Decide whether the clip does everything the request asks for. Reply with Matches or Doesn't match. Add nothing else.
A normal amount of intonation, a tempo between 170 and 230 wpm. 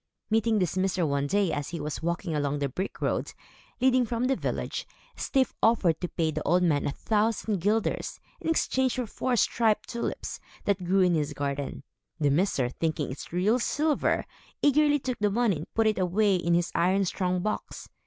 Doesn't match